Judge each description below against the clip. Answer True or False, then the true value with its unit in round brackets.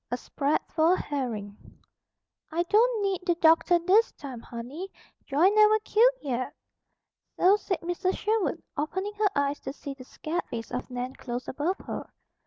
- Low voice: False (330 Hz)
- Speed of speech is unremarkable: True (165 wpm)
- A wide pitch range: True (6.5 semitones)